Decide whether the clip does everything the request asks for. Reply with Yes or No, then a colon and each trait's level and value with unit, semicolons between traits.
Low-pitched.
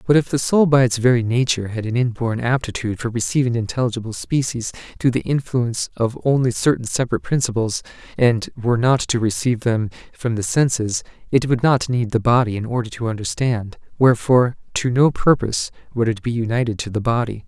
Yes: low, 120 Hz